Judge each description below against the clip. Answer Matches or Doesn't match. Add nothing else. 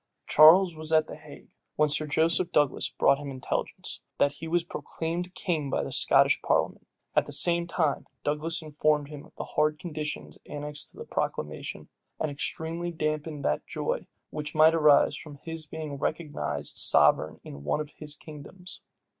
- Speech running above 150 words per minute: Matches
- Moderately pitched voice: Matches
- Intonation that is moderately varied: Doesn't match